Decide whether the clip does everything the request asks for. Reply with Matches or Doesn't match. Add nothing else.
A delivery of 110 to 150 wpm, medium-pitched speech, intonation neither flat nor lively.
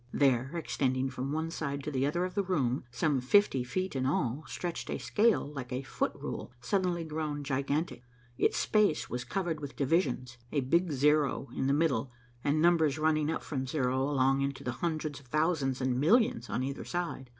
Doesn't match